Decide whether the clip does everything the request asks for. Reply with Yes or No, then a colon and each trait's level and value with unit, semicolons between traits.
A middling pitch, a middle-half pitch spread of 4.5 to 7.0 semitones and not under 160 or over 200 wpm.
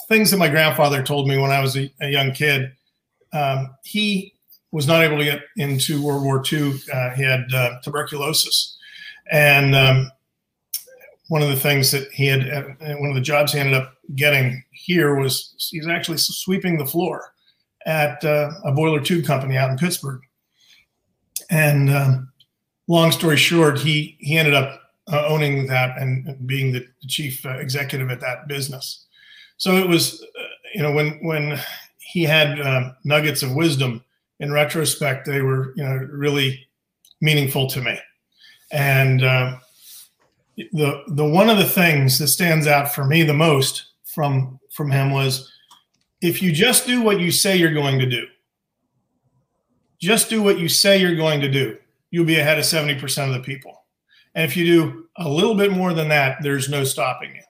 No: medium, 145 Hz; average, 3.2 semitones; average, 175 wpm